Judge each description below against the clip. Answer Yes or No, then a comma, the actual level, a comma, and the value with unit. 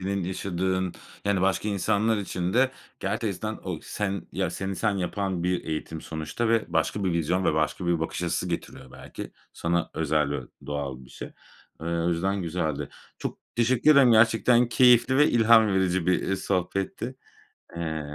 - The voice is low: Yes, very low, 95 Hz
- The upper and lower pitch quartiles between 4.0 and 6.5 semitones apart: Yes, average, 4.3 semitones